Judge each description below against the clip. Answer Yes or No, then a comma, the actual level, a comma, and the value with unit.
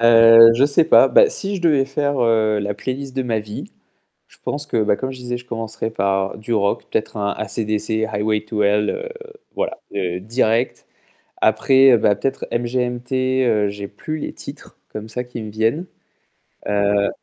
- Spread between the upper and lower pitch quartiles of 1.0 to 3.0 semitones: No, average, 3.7 semitones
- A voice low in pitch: Yes, low, 115 Hz